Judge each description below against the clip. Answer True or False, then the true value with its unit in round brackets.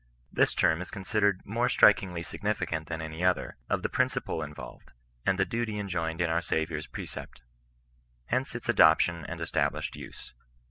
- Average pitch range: True (4.7 semitones)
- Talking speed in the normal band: True (155 wpm)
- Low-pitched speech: True (90 Hz)